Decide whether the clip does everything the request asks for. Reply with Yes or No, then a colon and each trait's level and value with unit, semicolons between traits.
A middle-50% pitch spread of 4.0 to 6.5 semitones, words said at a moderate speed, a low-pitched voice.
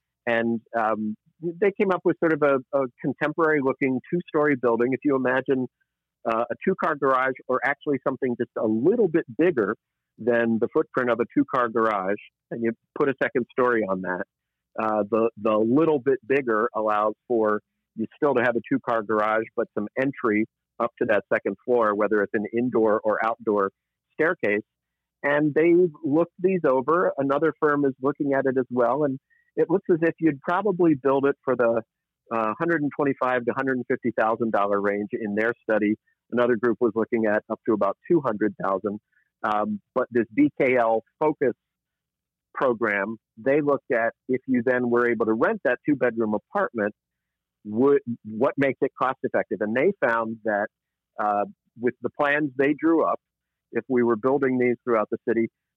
Yes: average, 4.4 semitones; average, 170 wpm; low, 125 Hz